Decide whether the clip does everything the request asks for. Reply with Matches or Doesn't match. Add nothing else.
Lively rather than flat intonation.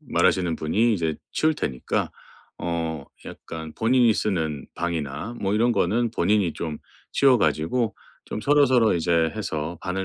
Matches